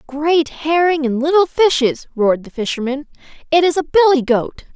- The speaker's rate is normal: Yes, average, 165 wpm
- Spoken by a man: No, female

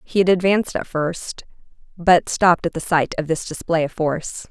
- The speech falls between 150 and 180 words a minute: No, average, 200 wpm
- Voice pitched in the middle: Yes, medium, 170 Hz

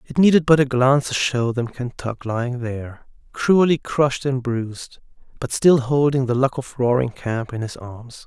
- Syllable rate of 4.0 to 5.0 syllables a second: Yes, 4.8 syllables/s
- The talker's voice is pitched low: Yes, low, 130 Hz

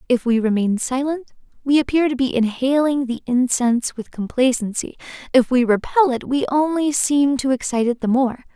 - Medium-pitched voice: No, very high, 260 Hz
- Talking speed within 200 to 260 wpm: No, average, 175 wpm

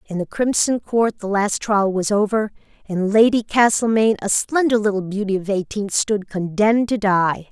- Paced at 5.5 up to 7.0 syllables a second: No, 4.9 syllables/s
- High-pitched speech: Yes, high, 210 Hz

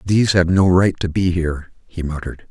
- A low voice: Yes, very low, 90 Hz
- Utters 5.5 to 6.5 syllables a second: Yes, 5.9 syllables/s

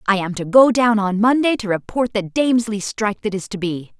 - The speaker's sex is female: Yes, female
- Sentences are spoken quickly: Yes, fast, 240 wpm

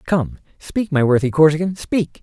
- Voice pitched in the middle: Yes, medium, 160 Hz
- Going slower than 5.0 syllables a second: Yes, 4.8 syllables/s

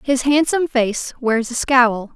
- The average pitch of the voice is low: No, very high, 255 Hz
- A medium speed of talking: Yes, average, 165 wpm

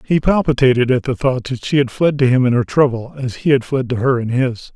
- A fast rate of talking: Yes, fast, 275 wpm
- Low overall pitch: Yes, low, 130 Hz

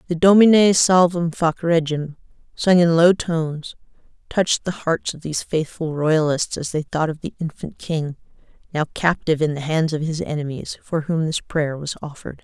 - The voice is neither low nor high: Yes, medium, 160 Hz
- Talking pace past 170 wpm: Yes, average, 180 wpm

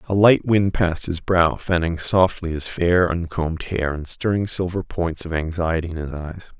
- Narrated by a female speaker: No, male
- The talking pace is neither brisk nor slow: Yes, average, 190 wpm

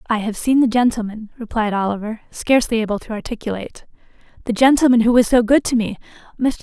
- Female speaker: Yes, female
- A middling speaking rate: Yes, average, 170 wpm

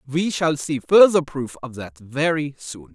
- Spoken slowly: No, average, 185 wpm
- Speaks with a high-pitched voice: No, medium, 140 Hz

